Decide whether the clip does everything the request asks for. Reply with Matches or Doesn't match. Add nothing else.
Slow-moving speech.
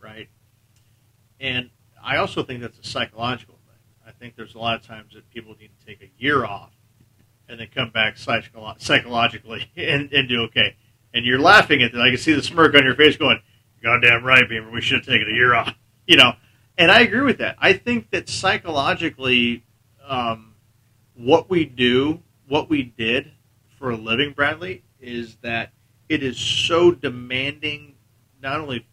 Doesn't match